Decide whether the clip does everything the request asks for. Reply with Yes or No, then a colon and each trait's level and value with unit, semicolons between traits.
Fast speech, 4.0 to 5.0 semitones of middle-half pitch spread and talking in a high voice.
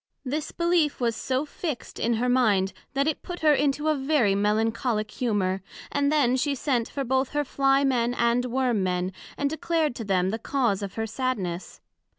No: average, 185 wpm; average, 4.7 semitones; very high, 250 Hz